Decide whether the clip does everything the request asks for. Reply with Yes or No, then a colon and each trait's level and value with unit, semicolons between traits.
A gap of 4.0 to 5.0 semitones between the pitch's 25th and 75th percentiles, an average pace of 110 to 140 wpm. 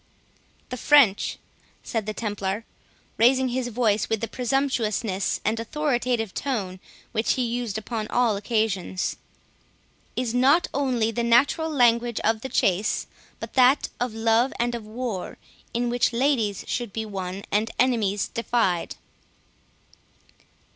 No: average, 2.7 semitones; slow, 135 wpm